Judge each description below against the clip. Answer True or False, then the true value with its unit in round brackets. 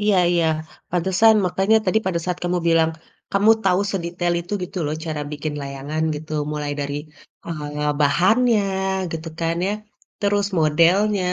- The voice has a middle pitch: True (170 Hz)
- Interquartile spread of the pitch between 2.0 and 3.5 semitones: False (4.0 semitones)